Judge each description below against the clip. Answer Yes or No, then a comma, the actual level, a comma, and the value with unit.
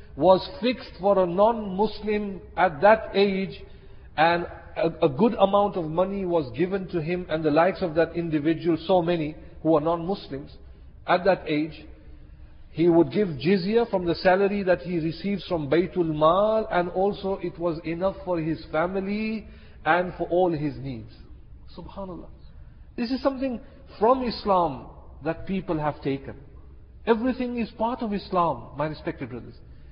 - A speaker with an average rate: Yes, average, 155 wpm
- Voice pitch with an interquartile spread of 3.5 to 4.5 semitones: Yes, average, 4.0 semitones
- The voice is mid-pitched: Yes, medium, 175 Hz